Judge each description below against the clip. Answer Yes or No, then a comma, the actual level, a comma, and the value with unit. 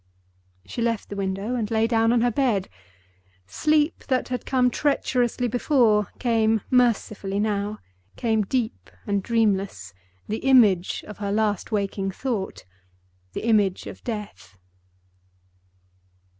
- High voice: Yes, high, 215 Hz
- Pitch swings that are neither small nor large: Yes, average, 3.6 semitones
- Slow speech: Yes, slow, 120 wpm